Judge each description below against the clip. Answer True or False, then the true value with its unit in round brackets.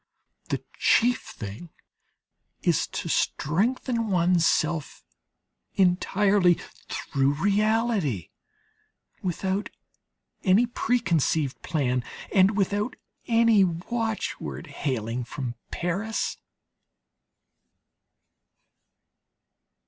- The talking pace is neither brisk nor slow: False (70 wpm)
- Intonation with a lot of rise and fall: True (6.4 semitones)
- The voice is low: False (185 Hz)